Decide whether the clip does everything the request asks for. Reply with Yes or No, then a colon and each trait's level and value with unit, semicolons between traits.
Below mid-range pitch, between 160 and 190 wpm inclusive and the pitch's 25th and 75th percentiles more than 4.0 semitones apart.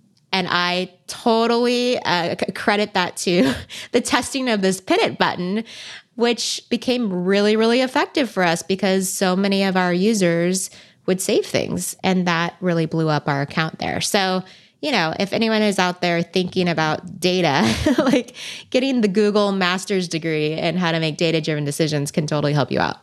No: medium, 185 Hz; average, 175 wpm; average, 4.5 semitones